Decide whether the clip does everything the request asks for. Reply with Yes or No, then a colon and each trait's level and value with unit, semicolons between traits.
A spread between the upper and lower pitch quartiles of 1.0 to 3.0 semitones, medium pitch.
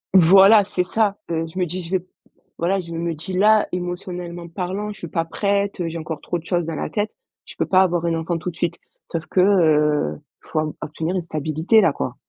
Yes: average, 2.7 semitones; medium, 175 Hz